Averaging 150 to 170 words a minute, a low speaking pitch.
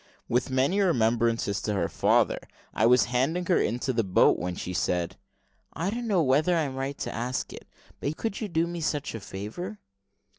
No: average, 195 wpm; low, 130 Hz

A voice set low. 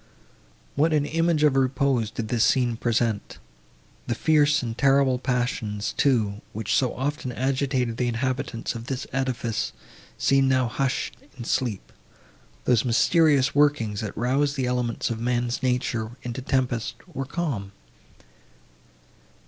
Yes: low, 125 Hz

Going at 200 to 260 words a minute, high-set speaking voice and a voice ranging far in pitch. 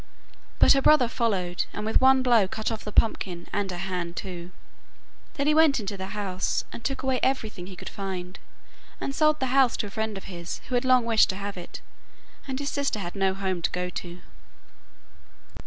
Yes: fast, 205 wpm; high, 210 Hz; wide, 5.7 semitones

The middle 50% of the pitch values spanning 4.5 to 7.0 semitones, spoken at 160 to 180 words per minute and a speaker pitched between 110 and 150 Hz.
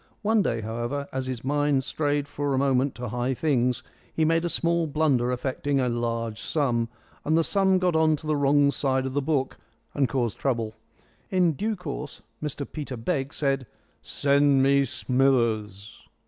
No: average, 3.3 semitones; average, 175 wpm; medium, 140 Hz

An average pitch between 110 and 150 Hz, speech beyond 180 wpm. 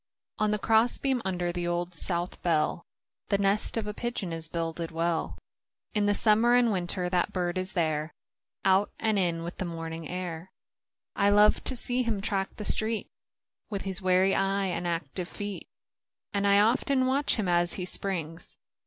No: high, 190 Hz; average, 190 wpm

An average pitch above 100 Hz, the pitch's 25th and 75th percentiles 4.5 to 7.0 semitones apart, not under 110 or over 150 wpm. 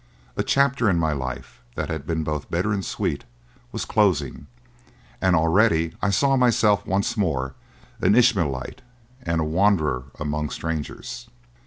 No: very low, 85 Hz; average, 5.3 semitones; average, 145 wpm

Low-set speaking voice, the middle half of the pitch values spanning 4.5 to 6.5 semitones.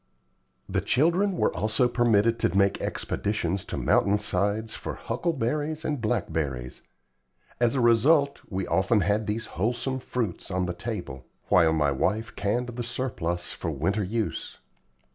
Yes: low, 110 Hz; average, 5.0 semitones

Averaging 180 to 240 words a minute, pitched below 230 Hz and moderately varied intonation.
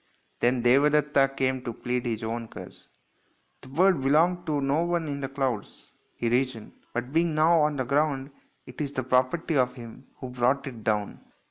Yes: average, 195 wpm; low, 135 Hz; average, 3.4 semitones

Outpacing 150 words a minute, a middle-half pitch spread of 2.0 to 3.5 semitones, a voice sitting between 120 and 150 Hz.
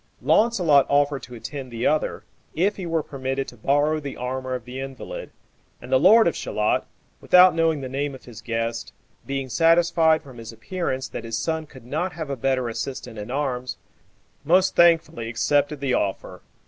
No: average, 180 wpm; average, 4.6 semitones; medium, 140 Hz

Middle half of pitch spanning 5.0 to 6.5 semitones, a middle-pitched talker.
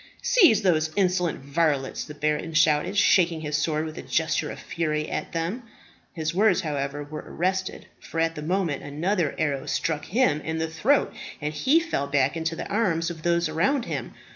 No: average, 3.2 semitones; medium, 160 Hz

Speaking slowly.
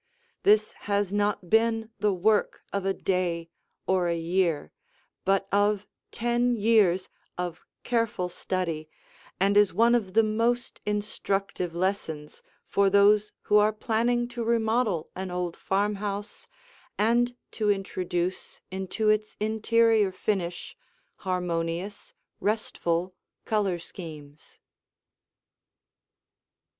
Yes: slow, 105 wpm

